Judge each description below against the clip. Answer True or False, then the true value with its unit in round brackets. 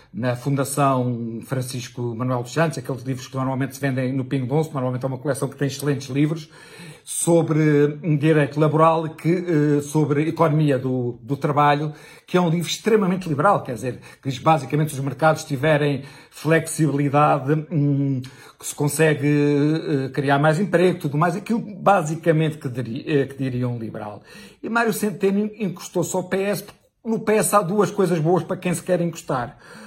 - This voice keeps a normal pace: True (165 wpm)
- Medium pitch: True (150 Hz)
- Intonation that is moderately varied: True (3.5 semitones)